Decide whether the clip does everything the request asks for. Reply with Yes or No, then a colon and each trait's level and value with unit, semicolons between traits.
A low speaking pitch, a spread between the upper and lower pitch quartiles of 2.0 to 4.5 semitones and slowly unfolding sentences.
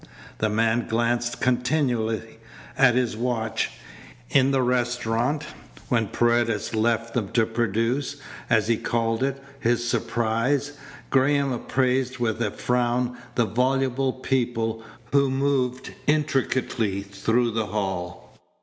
Yes: low, 120 Hz; narrow, 2.4 semitones; slow, 115 wpm